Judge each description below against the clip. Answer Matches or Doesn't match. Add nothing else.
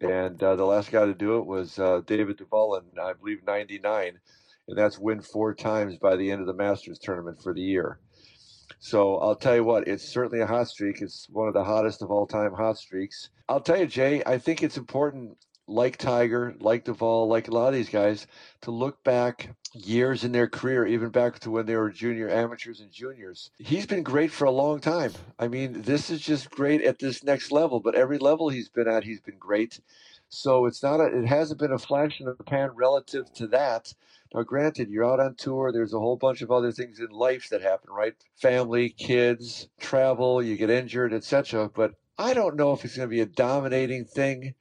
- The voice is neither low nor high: Doesn't match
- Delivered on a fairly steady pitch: Doesn't match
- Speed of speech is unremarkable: Doesn't match